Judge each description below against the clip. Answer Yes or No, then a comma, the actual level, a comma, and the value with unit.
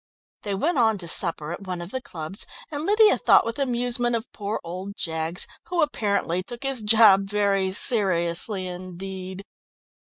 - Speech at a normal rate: Yes, average, 160 wpm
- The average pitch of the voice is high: Yes, high, 200 Hz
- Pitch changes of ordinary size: Yes, average, 4.6 semitones